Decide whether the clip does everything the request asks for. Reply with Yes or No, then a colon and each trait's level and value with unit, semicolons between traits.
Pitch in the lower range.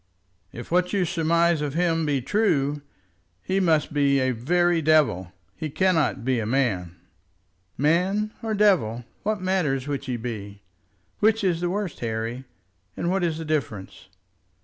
No: medium, 155 Hz